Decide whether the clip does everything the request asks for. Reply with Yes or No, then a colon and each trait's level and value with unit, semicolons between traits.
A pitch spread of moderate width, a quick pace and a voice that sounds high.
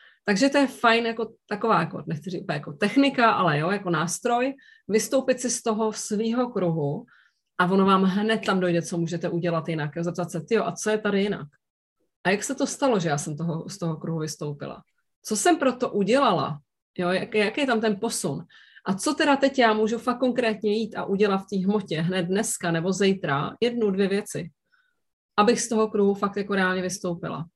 Yes: average, 4.7 semitones; fast, 200 wpm; high, 200 Hz